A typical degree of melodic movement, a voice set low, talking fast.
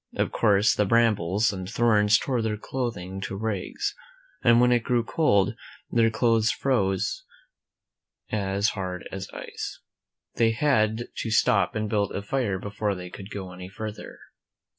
No: average, 3.1 semitones; low, 105 Hz; average, 155 wpm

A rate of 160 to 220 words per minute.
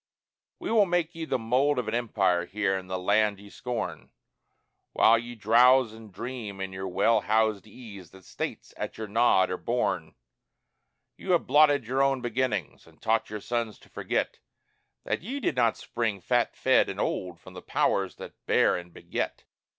Yes: average, 180 wpm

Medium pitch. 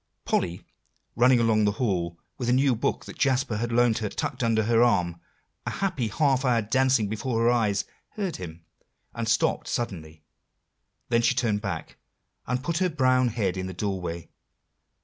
No: low, 115 Hz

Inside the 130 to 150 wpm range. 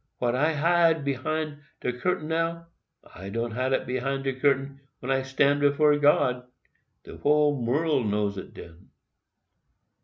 Yes: average, 145 wpm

